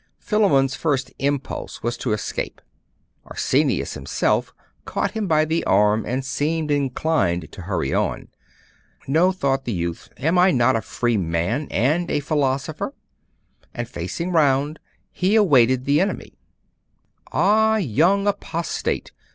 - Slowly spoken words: Yes, slow, 130 wpm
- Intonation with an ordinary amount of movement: No, wide, 5.7 semitones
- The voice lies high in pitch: No, medium, 140 Hz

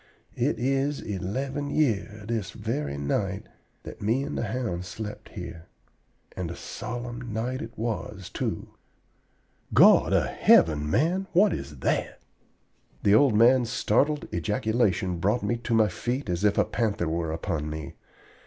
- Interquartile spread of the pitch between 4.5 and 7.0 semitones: Yes, wide, 5.5 semitones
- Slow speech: No, average, 145 wpm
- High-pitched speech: No, low, 110 Hz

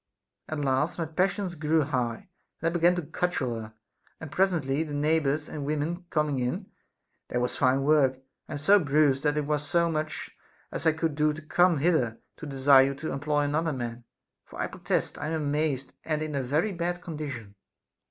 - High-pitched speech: No, medium, 150 Hz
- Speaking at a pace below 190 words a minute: No, average, 195 wpm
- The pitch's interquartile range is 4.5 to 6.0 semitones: No, average, 2.9 semitones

